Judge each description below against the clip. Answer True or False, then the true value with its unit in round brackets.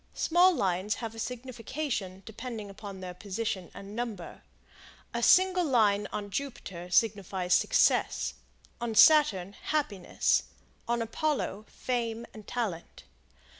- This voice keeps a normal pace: False (115 wpm)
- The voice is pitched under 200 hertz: False (220 Hz)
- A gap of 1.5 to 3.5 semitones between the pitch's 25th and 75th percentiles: False (4.0 semitones)